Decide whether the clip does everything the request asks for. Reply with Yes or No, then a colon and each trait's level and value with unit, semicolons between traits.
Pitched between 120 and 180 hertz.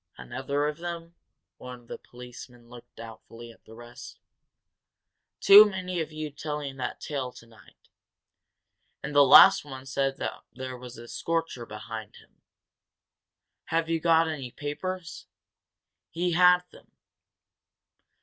Yes: medium, 140 Hz